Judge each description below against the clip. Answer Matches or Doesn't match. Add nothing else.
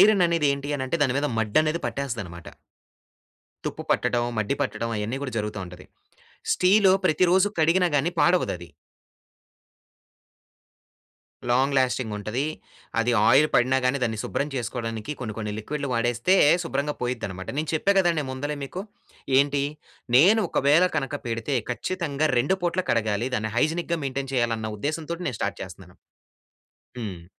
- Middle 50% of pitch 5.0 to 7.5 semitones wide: Matches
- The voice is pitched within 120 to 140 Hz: Matches